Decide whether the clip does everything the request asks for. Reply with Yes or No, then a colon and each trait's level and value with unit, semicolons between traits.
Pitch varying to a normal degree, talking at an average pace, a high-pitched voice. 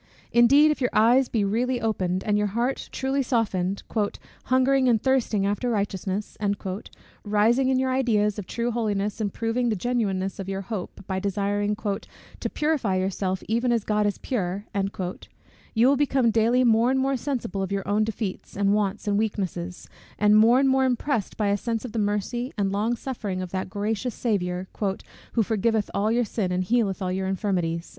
Yes: average, 3.6 semitones; average, 180 wpm; high, 215 Hz